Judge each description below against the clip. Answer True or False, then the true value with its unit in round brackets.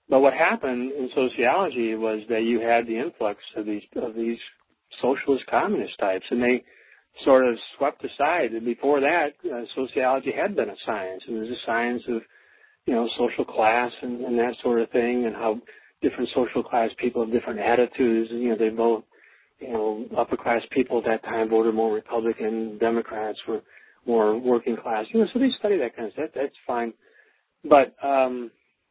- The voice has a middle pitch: False (120 Hz)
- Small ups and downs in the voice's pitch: True (1.8 semitones)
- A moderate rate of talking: True (195 wpm)